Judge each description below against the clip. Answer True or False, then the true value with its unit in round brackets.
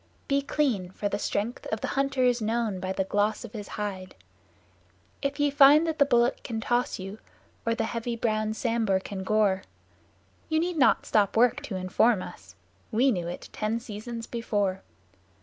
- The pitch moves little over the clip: False (3.6 semitones)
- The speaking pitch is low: False (225 Hz)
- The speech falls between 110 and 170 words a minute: False (180 wpm)